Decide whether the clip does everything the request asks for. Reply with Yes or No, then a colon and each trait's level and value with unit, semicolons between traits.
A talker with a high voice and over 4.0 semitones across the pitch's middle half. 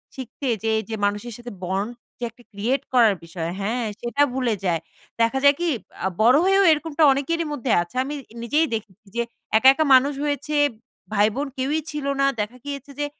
Yes: very high, 255 Hz; average, 4.8 semitones